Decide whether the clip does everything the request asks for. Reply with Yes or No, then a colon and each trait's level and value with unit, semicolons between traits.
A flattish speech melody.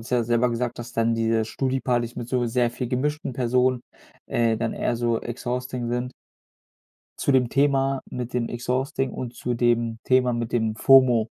Yes: narrow, 1.5 semitones